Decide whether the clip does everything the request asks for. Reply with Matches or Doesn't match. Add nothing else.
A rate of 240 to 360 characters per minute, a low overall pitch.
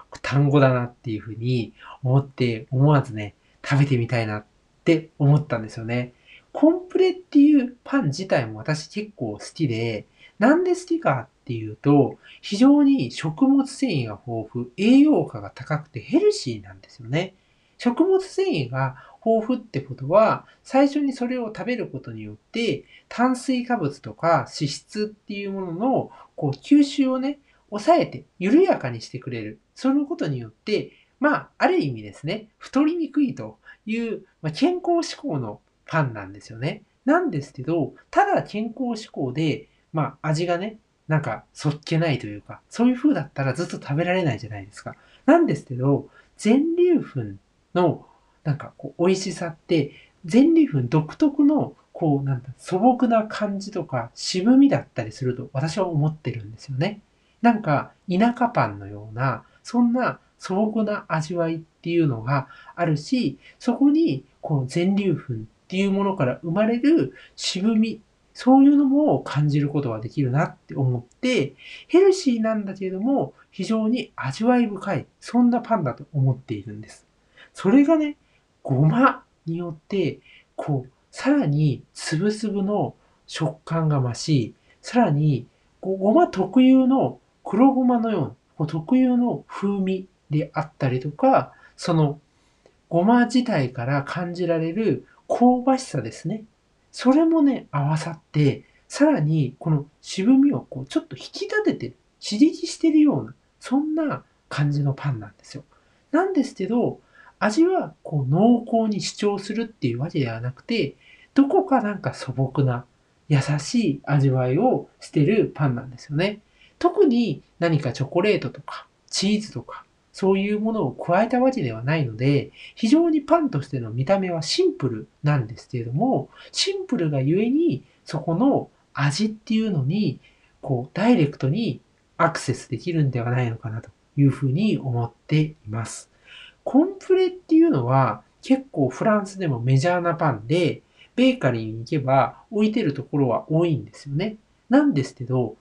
Doesn't match